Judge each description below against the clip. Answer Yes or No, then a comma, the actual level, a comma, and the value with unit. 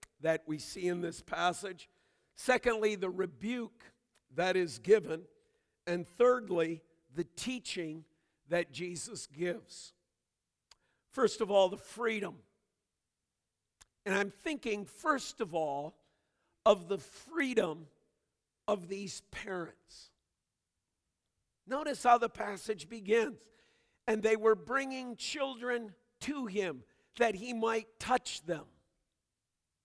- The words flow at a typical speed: No, slow, 105 wpm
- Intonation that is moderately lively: No, wide, 5.9 semitones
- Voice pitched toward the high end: Yes, high, 200 Hz